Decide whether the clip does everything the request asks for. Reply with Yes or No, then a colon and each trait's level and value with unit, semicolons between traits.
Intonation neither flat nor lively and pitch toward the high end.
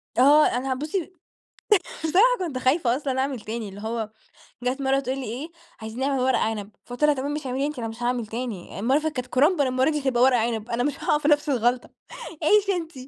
Yes: average, 3.6 semitones; very high, 260 Hz